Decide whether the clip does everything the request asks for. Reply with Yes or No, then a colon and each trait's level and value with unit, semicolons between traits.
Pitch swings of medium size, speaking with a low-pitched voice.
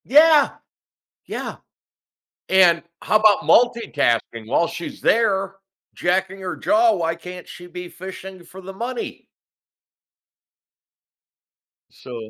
No: average, 3.8 semitones; high, 190 Hz